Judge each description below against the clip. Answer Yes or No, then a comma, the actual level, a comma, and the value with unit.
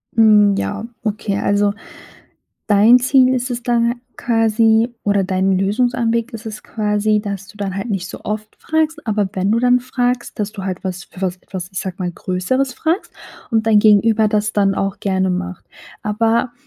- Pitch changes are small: No, average, 3.1 semitones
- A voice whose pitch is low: No, high, 215 Hz